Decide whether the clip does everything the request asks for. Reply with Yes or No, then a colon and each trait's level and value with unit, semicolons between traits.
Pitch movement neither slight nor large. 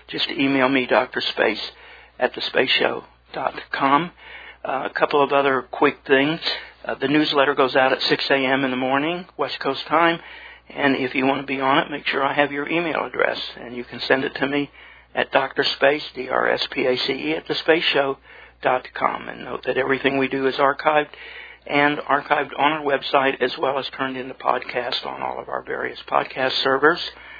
No: narrow, 1.7 semitones